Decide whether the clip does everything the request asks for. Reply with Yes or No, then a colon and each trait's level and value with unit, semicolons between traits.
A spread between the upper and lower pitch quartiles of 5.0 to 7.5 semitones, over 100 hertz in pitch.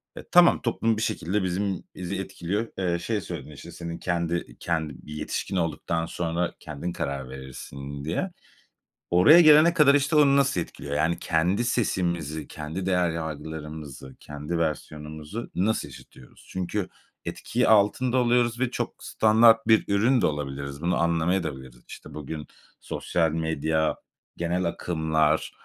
No: wide, 5.4 semitones; very low, 85 Hz